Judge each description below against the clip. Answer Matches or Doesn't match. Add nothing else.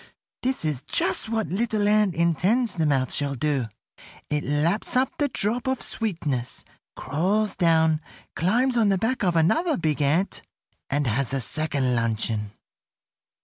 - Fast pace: Doesn't match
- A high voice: Doesn't match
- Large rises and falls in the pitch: Matches